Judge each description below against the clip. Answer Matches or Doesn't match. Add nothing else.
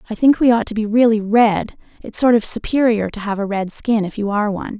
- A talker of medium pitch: Doesn't match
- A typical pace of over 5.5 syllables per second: Matches